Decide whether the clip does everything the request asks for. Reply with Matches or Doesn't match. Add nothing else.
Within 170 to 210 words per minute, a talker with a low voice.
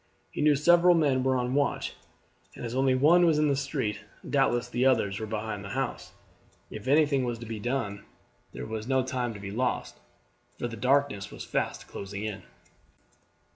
Matches